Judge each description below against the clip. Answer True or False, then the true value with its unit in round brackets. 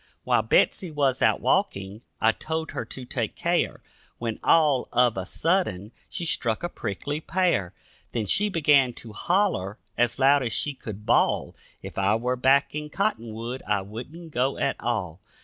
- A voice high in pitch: False (125 Hz)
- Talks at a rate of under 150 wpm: False (165 wpm)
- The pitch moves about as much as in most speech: False (5.8 semitones)